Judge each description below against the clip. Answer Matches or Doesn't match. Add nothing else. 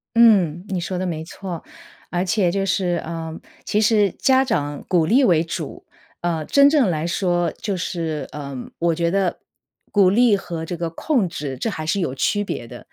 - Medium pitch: Matches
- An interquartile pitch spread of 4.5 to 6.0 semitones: Doesn't match